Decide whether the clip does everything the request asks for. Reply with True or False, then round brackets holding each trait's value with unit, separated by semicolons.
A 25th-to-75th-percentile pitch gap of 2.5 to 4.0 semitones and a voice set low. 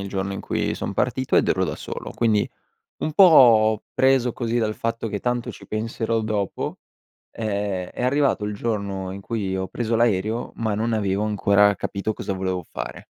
True (2.8 semitones; 110 Hz)